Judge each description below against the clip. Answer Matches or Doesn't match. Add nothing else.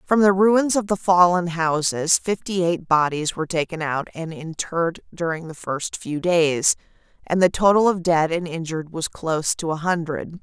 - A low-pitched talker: Doesn't match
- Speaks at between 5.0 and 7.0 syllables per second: Doesn't match